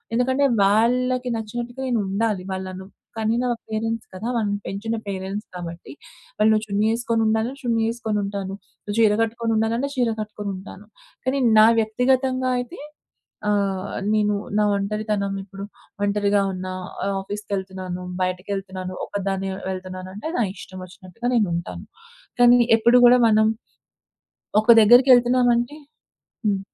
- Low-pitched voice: No, high, 215 Hz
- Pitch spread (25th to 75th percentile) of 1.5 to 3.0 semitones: No, average, 3.4 semitones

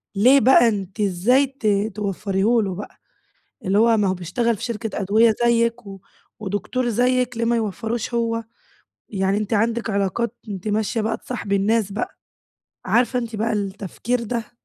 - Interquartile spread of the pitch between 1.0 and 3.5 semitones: Yes, average, 2.8 semitones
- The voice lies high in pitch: Yes, high, 220 Hz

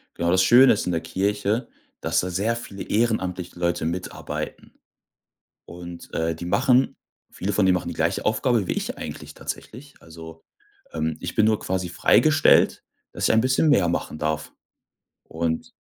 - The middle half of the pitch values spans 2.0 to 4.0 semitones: No, average, 4.7 semitones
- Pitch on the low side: Yes, very low, 95 Hz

